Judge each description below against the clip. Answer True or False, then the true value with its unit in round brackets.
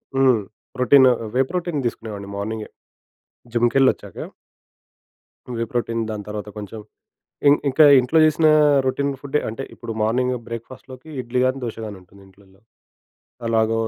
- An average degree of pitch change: True (3.4 semitones)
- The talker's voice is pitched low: True (120 Hz)